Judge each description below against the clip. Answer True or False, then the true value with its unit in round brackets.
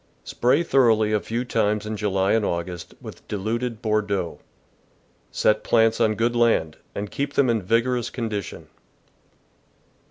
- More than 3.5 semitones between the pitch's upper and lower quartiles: False (2.4 semitones)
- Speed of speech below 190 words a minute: True (140 wpm)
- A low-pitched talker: True (110 Hz)